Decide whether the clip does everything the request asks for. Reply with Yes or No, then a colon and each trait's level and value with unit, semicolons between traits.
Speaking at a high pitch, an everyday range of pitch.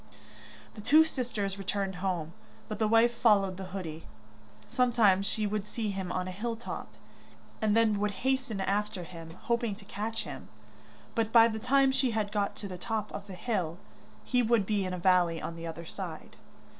Yes: high, 205 Hz; average, 3.6 semitones